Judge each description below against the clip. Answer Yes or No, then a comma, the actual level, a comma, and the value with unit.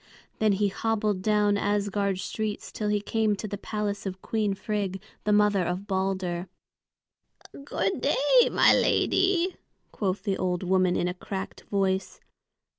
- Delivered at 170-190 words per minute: No, average, 145 wpm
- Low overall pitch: No, high, 205 Hz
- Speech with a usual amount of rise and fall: No, narrow, 1.9 semitones